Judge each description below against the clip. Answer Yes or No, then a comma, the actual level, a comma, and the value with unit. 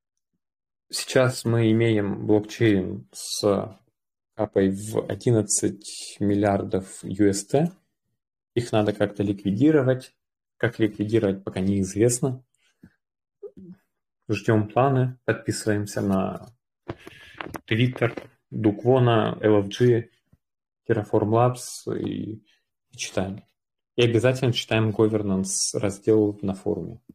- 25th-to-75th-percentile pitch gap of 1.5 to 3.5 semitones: Yes, average, 2.9 semitones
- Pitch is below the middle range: Yes, low, 110 Hz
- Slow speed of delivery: Yes, slow, 80 wpm